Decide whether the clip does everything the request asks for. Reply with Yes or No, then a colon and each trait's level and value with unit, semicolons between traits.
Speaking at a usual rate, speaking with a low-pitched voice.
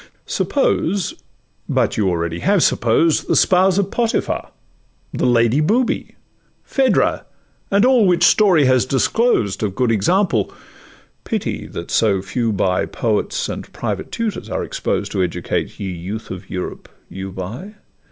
No: slow, 130 wpm; low, 125 Hz